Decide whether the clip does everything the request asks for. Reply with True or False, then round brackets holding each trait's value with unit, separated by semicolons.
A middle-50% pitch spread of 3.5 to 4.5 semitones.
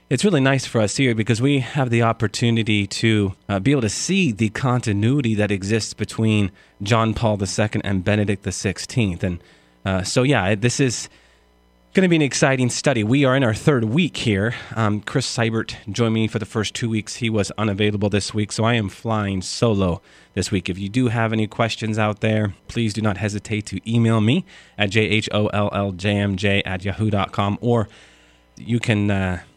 False (2.7 semitones)